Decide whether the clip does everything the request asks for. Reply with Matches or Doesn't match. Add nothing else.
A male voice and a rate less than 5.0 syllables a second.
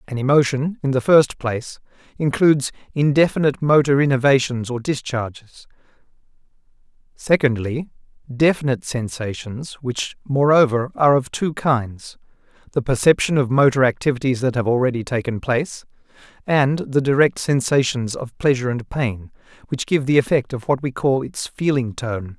Doesn't match